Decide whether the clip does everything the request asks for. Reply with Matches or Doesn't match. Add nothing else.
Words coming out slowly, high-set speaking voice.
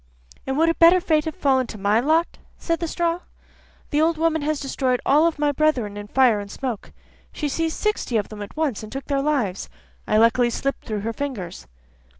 Doesn't match